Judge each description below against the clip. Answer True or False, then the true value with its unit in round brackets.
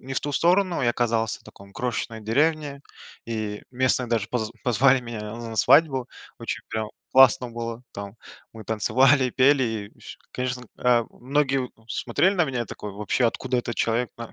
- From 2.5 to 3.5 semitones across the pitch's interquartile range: True (2.9 semitones)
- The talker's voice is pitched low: True (125 Hz)